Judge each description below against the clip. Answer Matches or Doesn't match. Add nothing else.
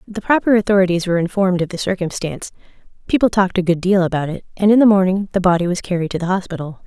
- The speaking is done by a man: Doesn't match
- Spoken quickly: Matches